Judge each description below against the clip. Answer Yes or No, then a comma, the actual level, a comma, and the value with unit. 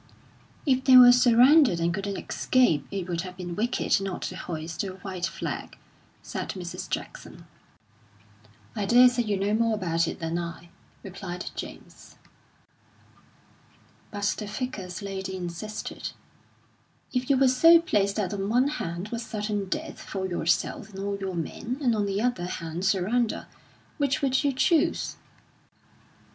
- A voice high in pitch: Yes, high, 200 Hz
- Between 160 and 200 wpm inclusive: No, average, 150 wpm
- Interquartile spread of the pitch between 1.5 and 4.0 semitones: No, average, 5.2 semitones